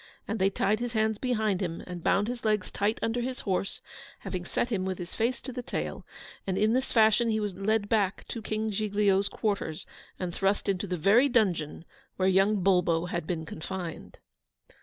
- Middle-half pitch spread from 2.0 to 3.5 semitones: Yes, average, 3.1 semitones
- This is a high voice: Yes, high, 205 Hz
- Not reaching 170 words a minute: No, average, 195 wpm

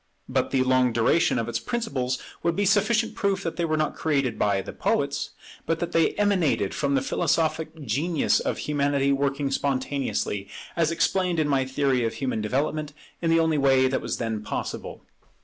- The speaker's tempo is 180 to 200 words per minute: Yes, average, 185 wpm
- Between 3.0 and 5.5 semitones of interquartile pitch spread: Yes, average, 4.2 semitones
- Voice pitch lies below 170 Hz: Yes, medium, 140 Hz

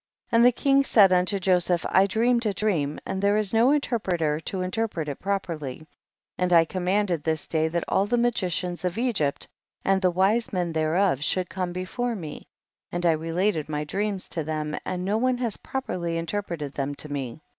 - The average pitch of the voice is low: No, medium, 185 Hz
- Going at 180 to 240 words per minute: Yes, average, 190 wpm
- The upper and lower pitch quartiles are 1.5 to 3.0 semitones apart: No, average, 4.5 semitones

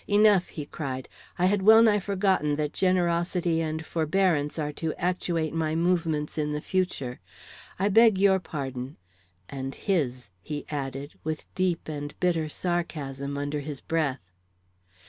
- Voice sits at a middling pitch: Yes, medium, 160 Hz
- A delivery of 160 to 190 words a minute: No, average, 140 wpm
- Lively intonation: No, average, 4.0 semitones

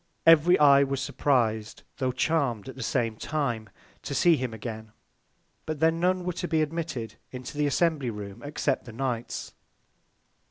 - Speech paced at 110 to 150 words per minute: No, average, 160 wpm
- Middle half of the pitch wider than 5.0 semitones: Yes, wide, 5.4 semitones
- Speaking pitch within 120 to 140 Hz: Yes, low, 135 Hz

